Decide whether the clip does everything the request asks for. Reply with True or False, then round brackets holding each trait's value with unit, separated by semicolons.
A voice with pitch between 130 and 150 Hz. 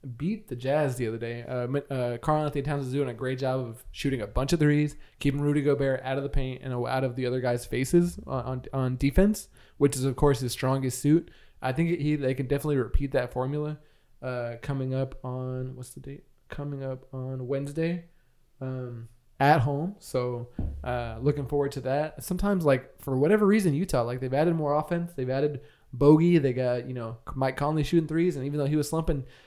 True (135 Hz)